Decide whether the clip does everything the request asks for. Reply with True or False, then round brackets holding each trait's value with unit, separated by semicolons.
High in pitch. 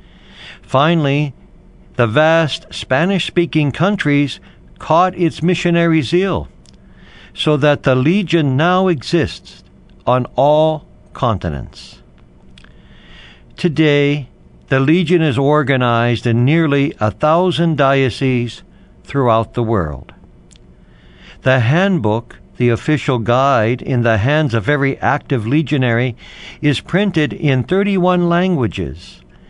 False (140 Hz)